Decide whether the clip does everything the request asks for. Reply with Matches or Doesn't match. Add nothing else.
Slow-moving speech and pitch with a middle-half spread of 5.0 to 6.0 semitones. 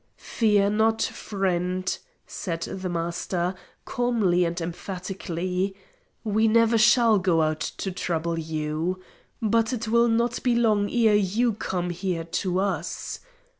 Doesn't match